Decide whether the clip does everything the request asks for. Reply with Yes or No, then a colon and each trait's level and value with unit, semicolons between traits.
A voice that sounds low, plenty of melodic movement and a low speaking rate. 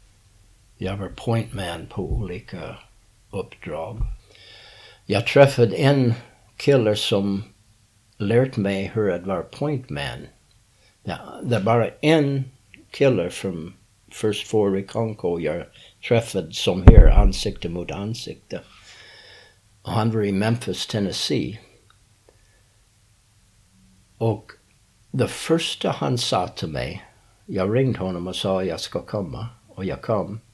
No: low, 105 Hz; average, 2.8 semitones; slow, 95 wpm